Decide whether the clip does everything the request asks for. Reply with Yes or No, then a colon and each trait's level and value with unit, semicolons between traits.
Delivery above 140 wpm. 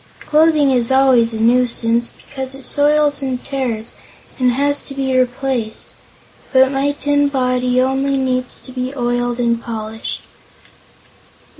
No: slow, 135 wpm